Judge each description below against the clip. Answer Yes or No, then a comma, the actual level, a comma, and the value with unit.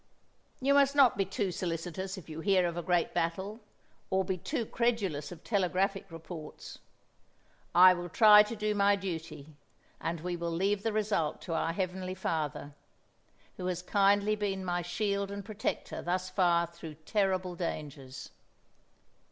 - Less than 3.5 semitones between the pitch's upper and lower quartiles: Yes, average, 3.1 semitones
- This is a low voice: No, medium, 185 Hz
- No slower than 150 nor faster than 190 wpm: Yes, average, 155 wpm